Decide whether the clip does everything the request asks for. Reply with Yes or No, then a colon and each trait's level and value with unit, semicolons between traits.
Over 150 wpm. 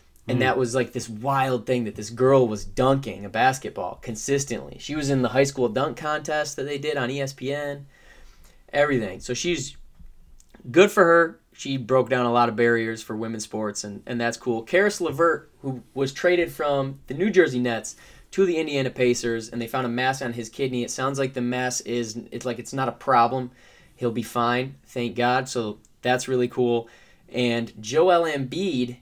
Yes: average, 195 wpm